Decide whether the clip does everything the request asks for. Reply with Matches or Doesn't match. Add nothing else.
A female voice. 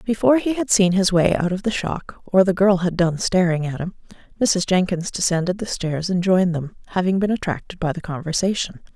Matches